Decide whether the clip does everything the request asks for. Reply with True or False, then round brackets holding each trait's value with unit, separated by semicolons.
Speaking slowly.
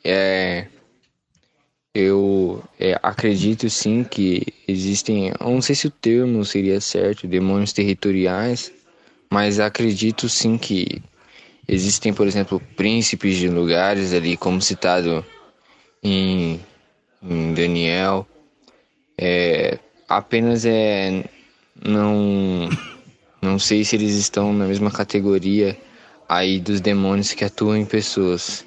True (105 wpm)